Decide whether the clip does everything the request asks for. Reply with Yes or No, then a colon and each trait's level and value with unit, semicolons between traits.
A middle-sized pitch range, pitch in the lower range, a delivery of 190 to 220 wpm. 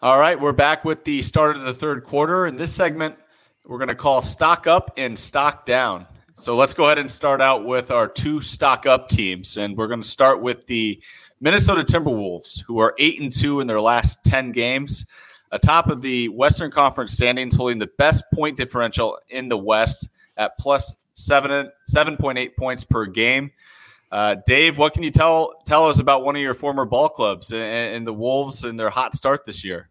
Yes: average, 3.6 semitones; low, 130 Hz; fast, 205 wpm